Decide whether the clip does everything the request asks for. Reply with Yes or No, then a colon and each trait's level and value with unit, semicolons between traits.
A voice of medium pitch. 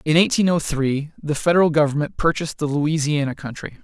Yes: medium, 155 Hz